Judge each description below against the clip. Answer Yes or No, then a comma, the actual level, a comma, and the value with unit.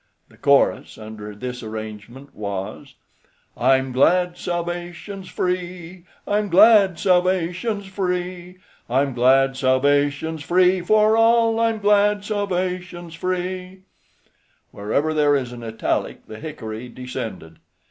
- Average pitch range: No, wide, 6.2 semitones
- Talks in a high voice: No, medium, 175 Hz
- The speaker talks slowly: Yes, slow, 105 wpm